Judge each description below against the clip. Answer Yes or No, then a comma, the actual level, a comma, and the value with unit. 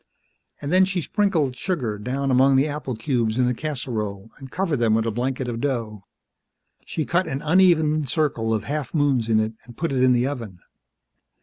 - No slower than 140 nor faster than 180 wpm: No, average, 195 wpm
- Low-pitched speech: Yes, low, 130 Hz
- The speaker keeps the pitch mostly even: No, average, 4.8 semitones